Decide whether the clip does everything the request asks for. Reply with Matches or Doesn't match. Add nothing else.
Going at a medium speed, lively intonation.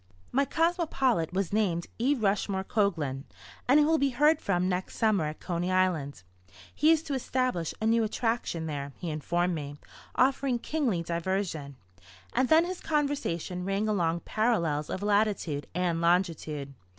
Matches